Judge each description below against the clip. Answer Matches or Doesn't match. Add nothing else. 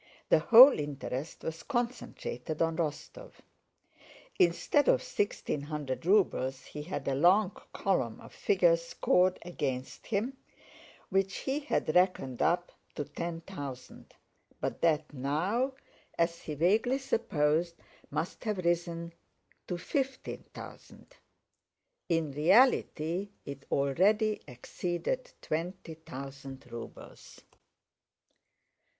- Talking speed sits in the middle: Doesn't match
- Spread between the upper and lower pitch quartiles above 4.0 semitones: Matches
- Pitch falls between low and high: Matches